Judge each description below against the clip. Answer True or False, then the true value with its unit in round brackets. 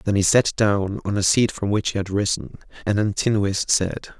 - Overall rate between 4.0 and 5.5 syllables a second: True (5.0 syllables/s)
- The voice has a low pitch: True (100 Hz)